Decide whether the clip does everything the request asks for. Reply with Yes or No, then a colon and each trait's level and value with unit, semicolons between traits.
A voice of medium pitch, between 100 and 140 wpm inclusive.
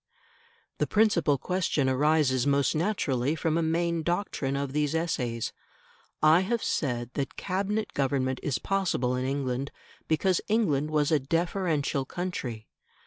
Yes: medium, 150 Hz; slow, 135 wpm